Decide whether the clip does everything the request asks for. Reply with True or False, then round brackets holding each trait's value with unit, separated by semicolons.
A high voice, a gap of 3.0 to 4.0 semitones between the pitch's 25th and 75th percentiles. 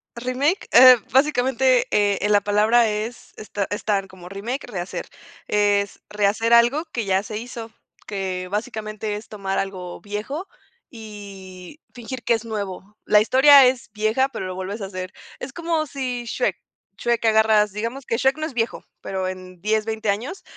True (215 Hz; 3.6 semitones)